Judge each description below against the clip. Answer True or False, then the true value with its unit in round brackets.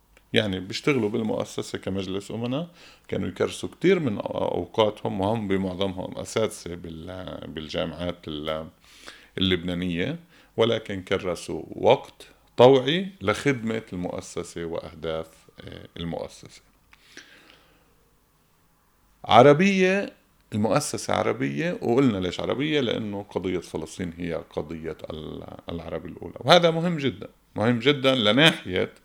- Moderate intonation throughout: False (6.9 semitones)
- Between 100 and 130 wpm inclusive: False (85 wpm)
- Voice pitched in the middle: False (100 Hz)